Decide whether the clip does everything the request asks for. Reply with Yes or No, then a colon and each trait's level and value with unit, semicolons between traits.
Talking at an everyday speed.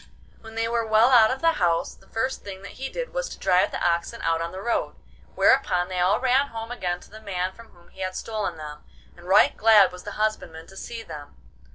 No: fast, 240 wpm